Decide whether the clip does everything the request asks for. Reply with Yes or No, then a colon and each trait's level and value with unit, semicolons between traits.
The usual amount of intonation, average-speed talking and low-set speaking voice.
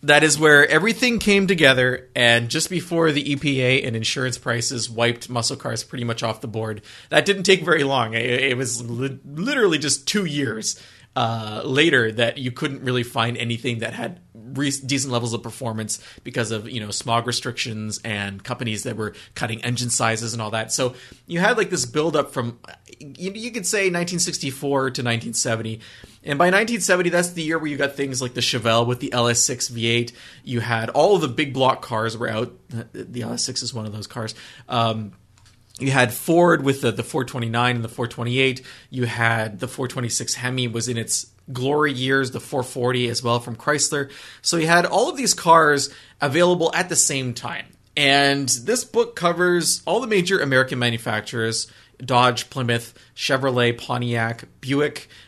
Yes: average, 3.8 semitones; average, 180 wpm; low, 125 Hz